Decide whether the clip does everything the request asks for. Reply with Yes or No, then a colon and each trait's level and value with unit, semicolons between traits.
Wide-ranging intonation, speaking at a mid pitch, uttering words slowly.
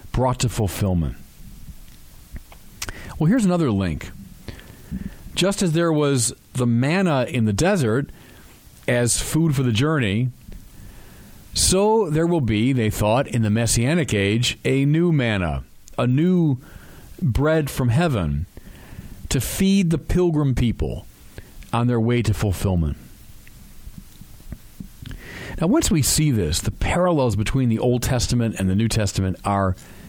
No: wide, 6.8 semitones; low, 120 Hz; slow, 130 wpm